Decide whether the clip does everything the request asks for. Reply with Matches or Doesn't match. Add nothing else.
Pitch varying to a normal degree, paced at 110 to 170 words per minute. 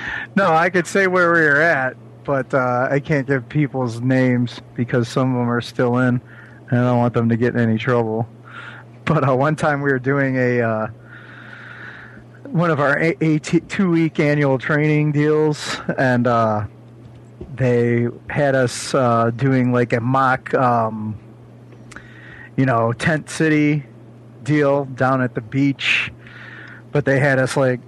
Matches